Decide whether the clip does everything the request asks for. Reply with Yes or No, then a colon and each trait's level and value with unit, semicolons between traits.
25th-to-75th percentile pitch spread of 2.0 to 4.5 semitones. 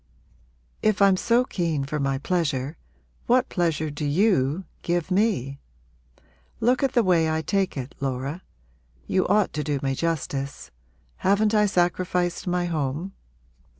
No: average, 5.2 semitones